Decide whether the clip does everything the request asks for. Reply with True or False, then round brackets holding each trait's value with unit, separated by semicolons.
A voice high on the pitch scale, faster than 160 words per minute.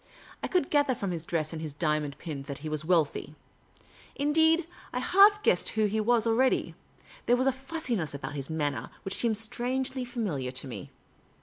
True (215 Hz; 185 wpm)